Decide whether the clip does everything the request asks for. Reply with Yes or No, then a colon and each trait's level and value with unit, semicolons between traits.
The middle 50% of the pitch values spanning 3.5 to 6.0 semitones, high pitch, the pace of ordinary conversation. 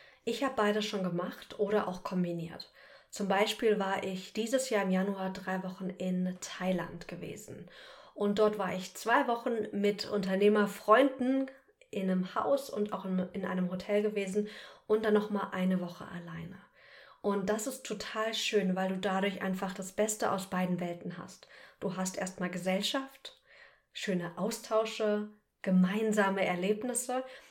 No: narrow, 2.4 semitones; high, 200 Hz; average, 145 wpm